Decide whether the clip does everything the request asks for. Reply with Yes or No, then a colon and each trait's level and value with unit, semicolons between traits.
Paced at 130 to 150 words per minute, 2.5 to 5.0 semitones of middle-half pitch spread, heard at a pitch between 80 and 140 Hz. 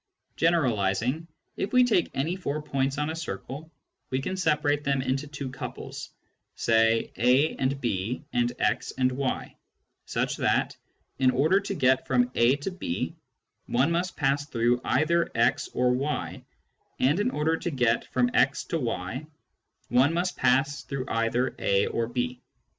No: average, 160 wpm; average, 3.8 semitones; low, 135 Hz